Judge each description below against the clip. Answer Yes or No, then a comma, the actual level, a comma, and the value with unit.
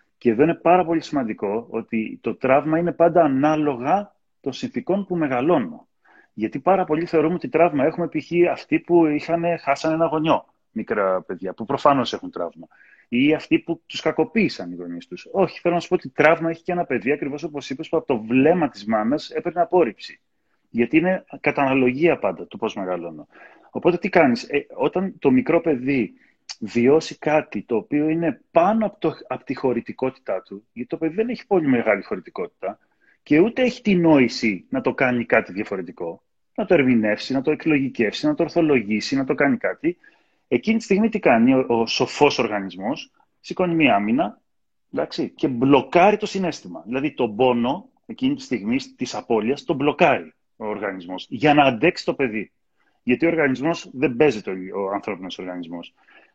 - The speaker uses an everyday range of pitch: No, wide, 5.8 semitones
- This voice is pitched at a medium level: Yes, medium, 155 Hz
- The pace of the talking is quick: Yes, fast, 175 wpm